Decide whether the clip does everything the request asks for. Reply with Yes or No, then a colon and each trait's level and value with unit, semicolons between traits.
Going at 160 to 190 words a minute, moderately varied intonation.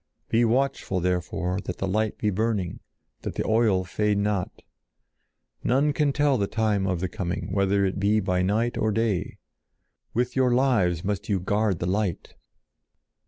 Yes: average, 165 wpm; average, 3.5 semitones